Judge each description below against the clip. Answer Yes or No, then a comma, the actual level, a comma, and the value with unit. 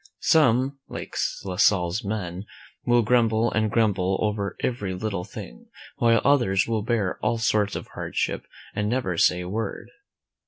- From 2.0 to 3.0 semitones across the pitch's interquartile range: No, average, 3.4 semitones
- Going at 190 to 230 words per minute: No, average, 150 wpm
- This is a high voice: No, low, 110 Hz